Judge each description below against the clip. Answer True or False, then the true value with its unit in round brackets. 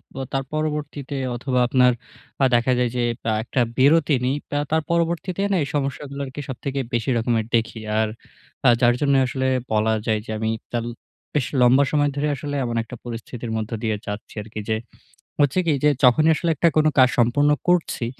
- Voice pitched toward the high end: False (130 Hz)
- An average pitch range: True (3.7 semitones)